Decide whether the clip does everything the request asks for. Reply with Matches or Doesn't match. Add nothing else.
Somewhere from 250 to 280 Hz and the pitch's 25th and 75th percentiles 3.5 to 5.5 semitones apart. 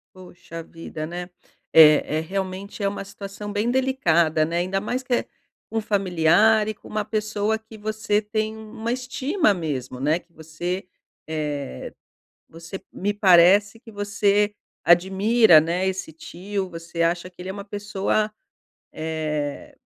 Doesn't match